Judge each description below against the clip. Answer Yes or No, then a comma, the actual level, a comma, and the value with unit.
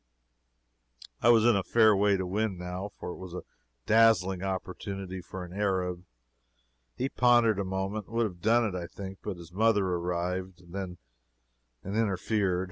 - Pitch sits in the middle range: No, very low, 95 Hz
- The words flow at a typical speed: Yes, average, 170 wpm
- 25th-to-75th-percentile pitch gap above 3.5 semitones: No, average, 3.1 semitones